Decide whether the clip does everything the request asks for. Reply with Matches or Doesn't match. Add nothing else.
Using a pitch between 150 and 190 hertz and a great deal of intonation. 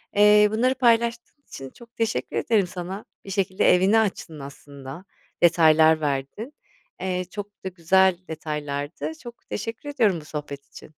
Matches